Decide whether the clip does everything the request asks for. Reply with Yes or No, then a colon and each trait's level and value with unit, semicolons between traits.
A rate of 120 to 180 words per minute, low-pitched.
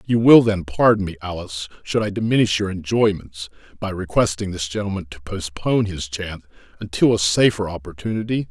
Yes: average, 160 wpm; very low, 95 Hz